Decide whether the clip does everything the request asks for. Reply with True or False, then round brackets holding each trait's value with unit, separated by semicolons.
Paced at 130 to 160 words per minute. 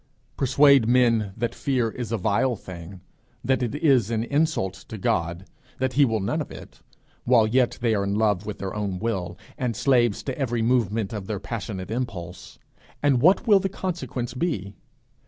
False (175 wpm)